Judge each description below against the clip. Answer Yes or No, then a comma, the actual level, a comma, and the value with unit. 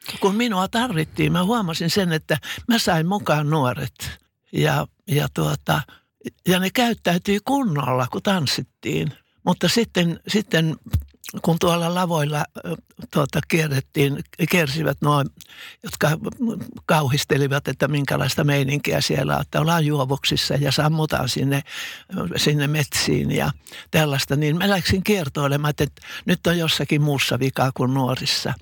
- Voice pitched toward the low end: No, medium, 155 Hz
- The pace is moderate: Yes, average, 120 wpm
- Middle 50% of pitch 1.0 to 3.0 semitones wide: No, average, 4.3 semitones